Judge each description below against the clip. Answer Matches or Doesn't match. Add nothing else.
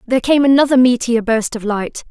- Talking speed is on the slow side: Doesn't match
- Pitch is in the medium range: Doesn't match